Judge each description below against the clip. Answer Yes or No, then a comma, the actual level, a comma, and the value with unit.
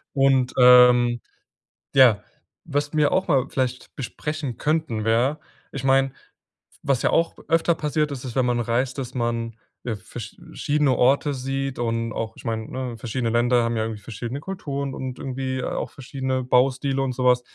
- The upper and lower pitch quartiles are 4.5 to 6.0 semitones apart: No, narrow, 2.4 semitones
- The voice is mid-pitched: No, low, 130 Hz